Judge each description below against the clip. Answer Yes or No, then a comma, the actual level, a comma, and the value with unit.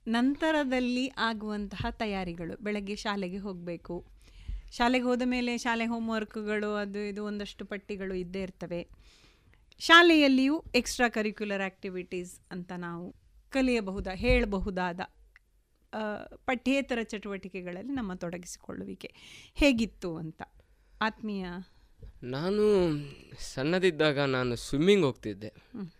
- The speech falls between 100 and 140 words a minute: No, average, 85 wpm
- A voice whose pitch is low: No, high, 205 Hz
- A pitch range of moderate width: Yes, average, 4.5 semitones